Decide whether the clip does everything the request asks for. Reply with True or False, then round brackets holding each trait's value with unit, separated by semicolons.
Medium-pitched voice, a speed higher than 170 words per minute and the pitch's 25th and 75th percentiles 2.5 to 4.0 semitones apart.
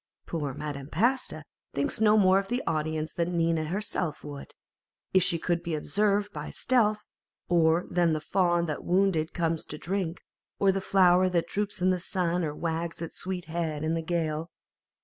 True (170 Hz; 180 wpm; 3.0 semitones)